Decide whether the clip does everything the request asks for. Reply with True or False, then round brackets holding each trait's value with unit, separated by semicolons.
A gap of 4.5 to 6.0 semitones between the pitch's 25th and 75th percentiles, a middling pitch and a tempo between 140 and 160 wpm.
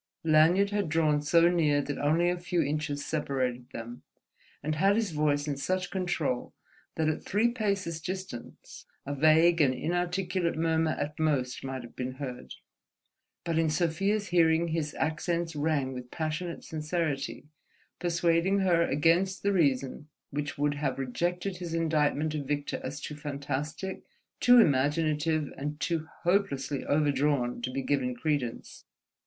False (3.3 semitones; 155 Hz; 145 wpm)